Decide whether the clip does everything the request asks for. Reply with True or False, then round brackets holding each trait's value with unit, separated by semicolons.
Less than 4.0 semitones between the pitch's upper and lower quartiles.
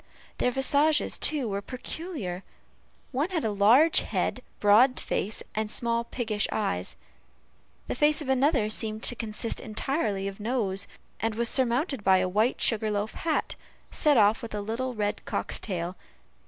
False (4.3 semitones)